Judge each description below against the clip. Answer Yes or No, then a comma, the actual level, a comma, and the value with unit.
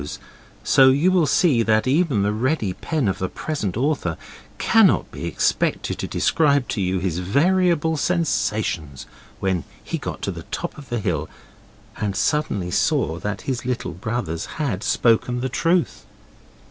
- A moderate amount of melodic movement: No, wide, 8.0 semitones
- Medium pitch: No, low, 120 Hz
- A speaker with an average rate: Yes, average, 160 wpm